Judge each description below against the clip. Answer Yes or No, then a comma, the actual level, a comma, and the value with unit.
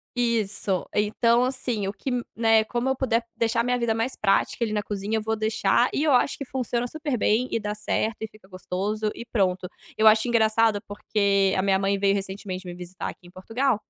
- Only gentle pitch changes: No, average, 3.0 semitones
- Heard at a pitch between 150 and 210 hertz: No, high, 220 Hz